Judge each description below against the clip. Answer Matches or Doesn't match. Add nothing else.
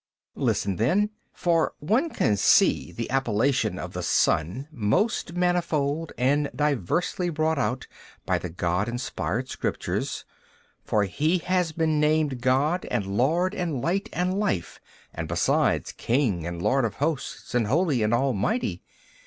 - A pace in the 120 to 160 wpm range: Matches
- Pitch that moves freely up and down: Matches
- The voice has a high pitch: Doesn't match